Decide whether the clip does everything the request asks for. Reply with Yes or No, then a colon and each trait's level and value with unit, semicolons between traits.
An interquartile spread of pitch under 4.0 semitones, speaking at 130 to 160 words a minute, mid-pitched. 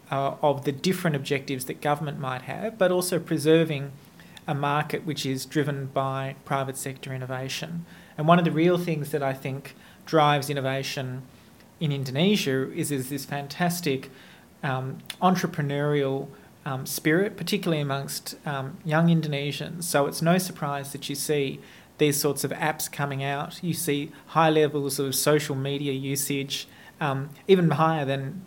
Yes: average, 2.8 semitones; average, 150 wpm; medium, 145 Hz